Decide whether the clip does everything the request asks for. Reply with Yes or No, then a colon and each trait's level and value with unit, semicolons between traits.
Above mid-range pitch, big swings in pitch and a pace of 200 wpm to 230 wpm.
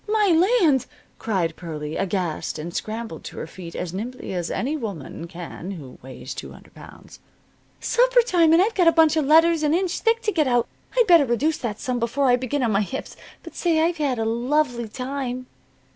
Yes: very high, 255 Hz; wide, 8.5 semitones; fast, 205 wpm